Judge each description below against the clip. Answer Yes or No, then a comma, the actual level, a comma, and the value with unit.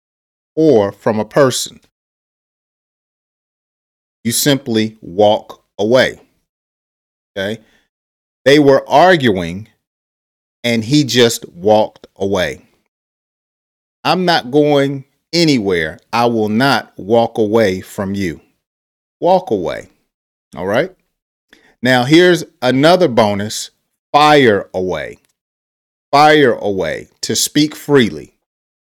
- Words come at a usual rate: No, slow, 90 wpm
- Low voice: Yes, low, 115 Hz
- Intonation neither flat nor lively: No, wide, 6.1 semitones